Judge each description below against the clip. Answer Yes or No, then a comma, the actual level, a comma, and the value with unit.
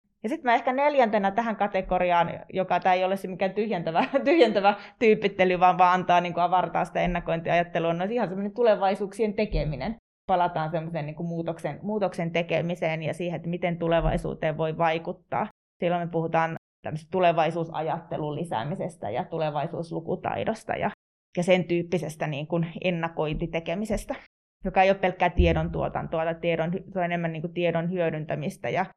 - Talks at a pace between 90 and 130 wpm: No, average, 145 wpm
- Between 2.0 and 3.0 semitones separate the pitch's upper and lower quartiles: Yes, narrow, 2.6 semitones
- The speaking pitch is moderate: Yes, medium, 175 Hz